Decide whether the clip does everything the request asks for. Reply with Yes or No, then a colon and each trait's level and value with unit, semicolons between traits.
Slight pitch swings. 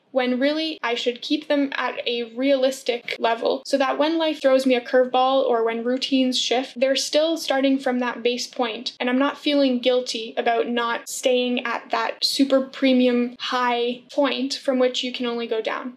Yes: narrow, 1.9 semitones